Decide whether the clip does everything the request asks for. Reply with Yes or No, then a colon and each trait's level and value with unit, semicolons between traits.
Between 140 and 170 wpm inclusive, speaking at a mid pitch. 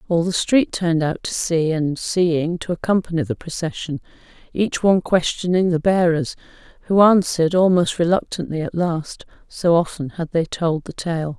Yes: average, 165 wpm; medium, 170 Hz